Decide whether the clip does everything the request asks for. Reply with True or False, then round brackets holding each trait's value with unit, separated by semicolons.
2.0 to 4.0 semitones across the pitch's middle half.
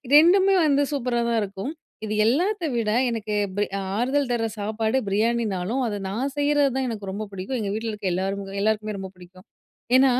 False (4.7 semitones)